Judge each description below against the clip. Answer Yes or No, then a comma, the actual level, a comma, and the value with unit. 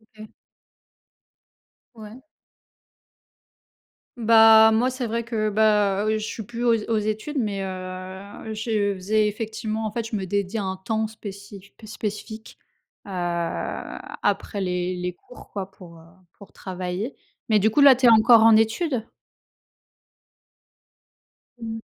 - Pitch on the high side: Yes, high, 215 Hz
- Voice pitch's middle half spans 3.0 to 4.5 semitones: No, narrow, 2.4 semitones